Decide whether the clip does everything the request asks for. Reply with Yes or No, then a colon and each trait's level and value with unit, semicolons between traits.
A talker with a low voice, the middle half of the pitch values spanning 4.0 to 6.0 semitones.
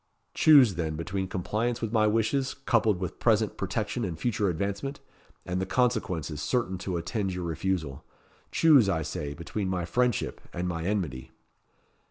Yes: very low, 95 Hz; average, 4.8 semitones